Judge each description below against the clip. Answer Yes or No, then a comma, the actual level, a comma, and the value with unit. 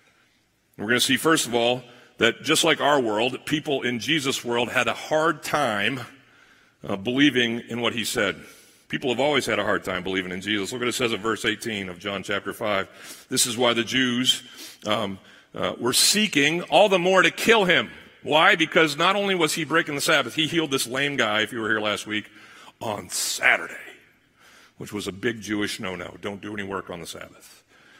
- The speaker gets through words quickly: Yes, fast, 210 wpm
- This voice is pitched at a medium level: No, low, 120 Hz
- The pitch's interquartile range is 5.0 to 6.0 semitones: Yes, wide, 5.4 semitones